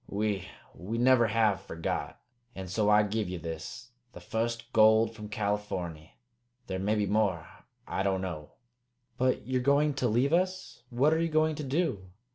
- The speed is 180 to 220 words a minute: No, average, 170 wpm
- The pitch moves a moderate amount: Yes, average, 4.9 semitones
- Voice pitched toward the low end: Yes, low, 110 Hz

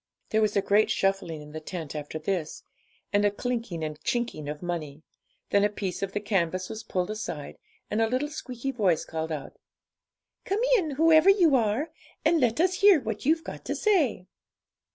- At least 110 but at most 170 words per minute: No, average, 190 wpm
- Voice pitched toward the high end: Yes, high, 205 Hz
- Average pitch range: No, wide, 7.7 semitones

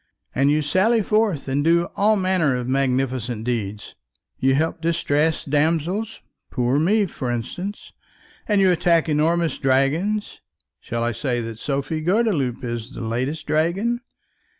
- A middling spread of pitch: No, wide, 5.9 semitones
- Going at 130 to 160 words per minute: Yes, average, 140 wpm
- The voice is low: No, medium, 150 Hz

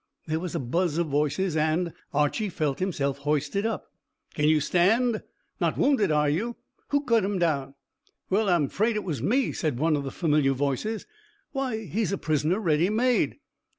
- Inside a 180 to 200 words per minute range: Yes, average, 185 wpm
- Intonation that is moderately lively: No, wide, 6.3 semitones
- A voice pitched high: No, medium, 170 Hz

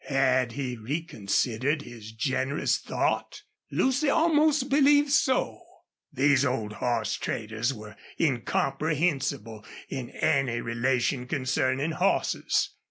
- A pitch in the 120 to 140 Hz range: Yes, low, 135 Hz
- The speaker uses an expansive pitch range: No, average, 5.0 semitones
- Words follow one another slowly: Yes, slow, 100 wpm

